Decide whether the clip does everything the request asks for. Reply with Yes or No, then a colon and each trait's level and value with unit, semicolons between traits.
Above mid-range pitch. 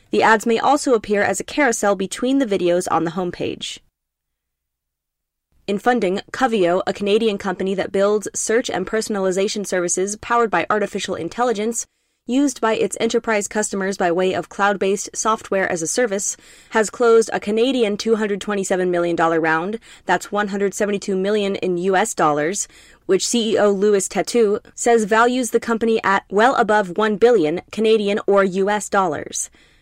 Yes: high, 200 Hz